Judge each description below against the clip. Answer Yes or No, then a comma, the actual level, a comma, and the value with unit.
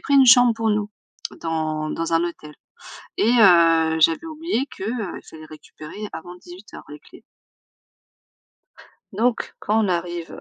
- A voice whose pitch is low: No, medium, 180 Hz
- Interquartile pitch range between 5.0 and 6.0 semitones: Yes, wide, 5.4 semitones